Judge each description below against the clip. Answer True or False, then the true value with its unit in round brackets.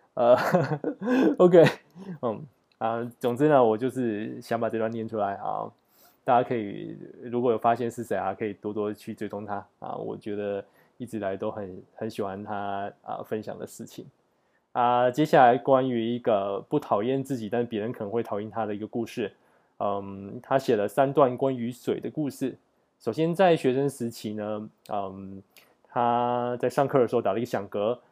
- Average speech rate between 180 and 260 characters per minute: False (285 characters per minute)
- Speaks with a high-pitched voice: False (115 Hz)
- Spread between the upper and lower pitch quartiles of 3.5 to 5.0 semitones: True (4.1 semitones)